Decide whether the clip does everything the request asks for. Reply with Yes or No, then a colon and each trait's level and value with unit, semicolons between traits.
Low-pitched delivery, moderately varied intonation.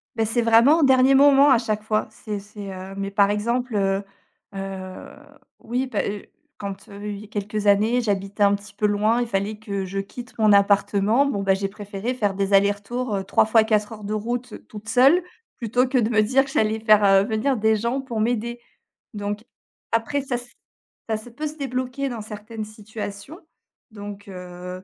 No: high, 215 Hz; average, 3.1 semitones